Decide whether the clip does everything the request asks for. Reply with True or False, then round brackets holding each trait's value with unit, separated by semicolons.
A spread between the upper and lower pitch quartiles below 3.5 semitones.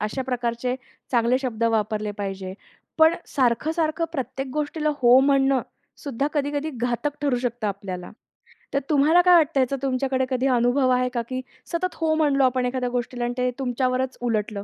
True (2.9 semitones)